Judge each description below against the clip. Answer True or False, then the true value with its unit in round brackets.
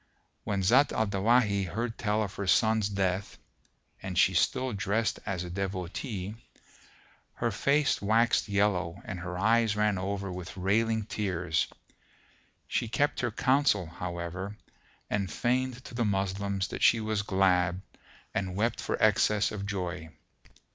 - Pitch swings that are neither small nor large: True (3.1 semitones)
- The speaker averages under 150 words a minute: True (140 wpm)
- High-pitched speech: False (100 Hz)